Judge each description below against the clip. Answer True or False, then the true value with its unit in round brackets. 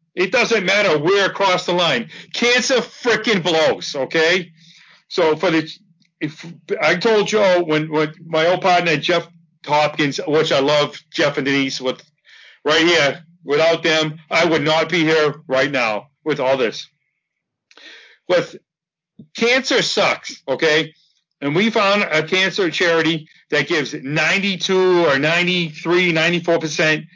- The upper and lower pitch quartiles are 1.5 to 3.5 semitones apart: True (2.9 semitones)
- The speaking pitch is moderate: True (165 Hz)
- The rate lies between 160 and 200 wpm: False (140 wpm)